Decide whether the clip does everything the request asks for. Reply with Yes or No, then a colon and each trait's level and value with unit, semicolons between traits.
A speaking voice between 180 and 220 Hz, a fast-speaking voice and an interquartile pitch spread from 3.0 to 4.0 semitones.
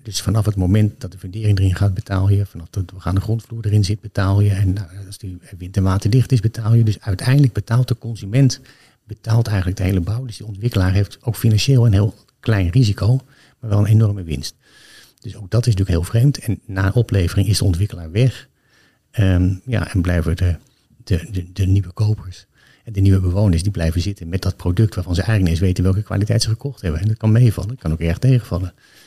No: low, 100 Hz; fast, 225 wpm; average, 3.3 semitones